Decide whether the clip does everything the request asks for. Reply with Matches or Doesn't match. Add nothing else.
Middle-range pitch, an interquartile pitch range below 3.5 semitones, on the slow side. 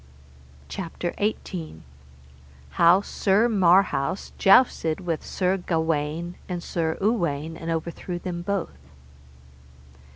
Matches